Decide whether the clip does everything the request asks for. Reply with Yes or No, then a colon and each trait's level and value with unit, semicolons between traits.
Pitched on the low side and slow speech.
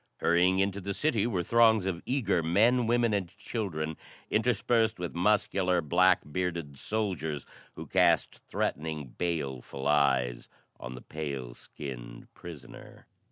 Yes: very low, 90 Hz; slow, 125 wpm